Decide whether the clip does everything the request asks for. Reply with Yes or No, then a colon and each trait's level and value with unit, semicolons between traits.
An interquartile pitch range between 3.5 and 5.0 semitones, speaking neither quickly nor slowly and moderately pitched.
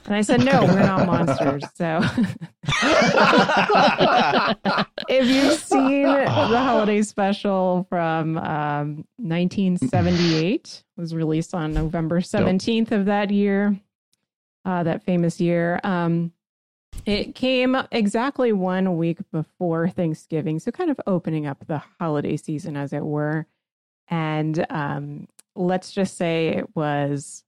No: average, 4.3 semitones; slow, 120 wpm; medium, 180 Hz